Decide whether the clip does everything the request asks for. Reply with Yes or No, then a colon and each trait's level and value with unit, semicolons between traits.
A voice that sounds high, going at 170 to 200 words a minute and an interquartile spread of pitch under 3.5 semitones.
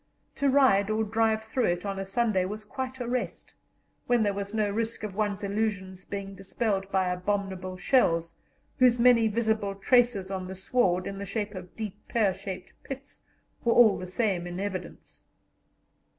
Yes: high, 205 Hz; average, 175 wpm; average, 3.1 semitones